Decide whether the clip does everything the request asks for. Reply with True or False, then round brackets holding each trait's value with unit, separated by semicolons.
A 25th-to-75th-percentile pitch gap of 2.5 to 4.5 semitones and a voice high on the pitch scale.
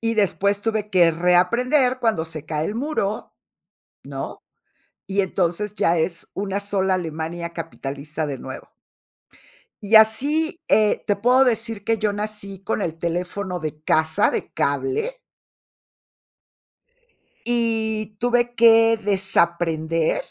False (5.0 semitones; 200 Hz)